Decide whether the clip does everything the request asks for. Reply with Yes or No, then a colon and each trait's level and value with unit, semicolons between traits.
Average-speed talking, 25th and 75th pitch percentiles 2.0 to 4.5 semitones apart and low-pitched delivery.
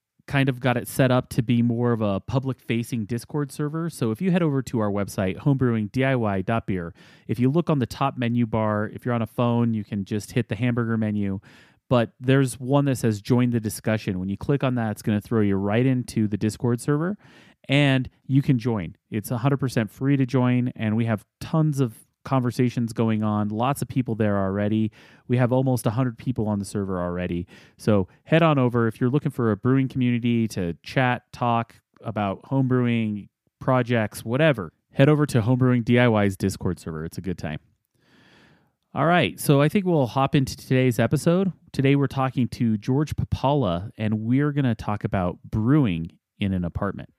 Yes: average, 195 wpm; average, 3.8 semitones; low, 120 Hz